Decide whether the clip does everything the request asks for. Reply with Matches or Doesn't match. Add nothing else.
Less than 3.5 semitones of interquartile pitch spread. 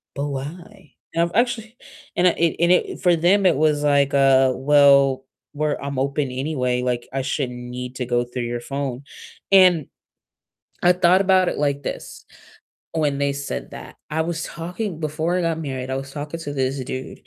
Doesn't match